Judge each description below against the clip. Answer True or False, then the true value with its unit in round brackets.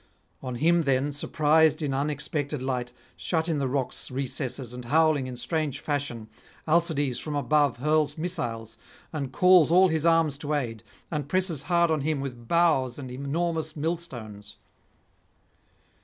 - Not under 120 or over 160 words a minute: True (145 wpm)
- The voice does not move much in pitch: False (3.7 semitones)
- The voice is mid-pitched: True (145 Hz)